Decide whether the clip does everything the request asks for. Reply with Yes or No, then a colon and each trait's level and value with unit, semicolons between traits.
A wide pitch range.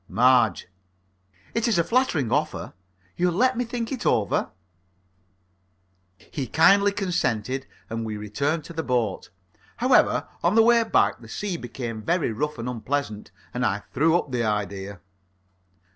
Yes: wide, 8.1 semitones